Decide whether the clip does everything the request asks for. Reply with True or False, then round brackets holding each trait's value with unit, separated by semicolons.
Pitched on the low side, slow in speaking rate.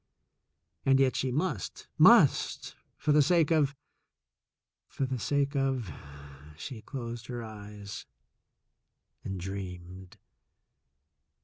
True (120 Hz; 110 wpm)